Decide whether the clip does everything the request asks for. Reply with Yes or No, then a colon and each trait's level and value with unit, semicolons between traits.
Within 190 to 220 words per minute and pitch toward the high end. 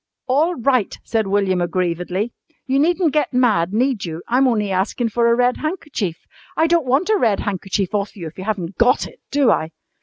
Yes: average, 195 wpm; high, 225 Hz